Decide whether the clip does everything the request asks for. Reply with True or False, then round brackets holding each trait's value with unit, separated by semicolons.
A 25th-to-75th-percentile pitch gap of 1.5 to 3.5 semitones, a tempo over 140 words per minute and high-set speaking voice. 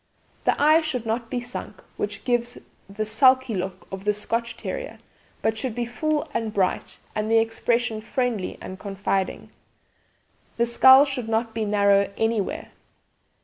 True (2.8 semitones; 150 wpm; 225 Hz)